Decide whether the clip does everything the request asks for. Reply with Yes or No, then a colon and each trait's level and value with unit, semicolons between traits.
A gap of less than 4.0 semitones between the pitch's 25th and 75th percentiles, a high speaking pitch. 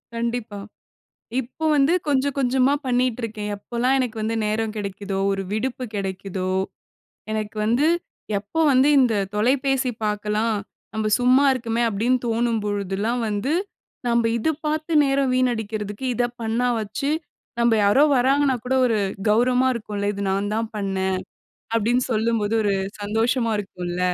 Yes: average, 3.5 semitones; high, 230 Hz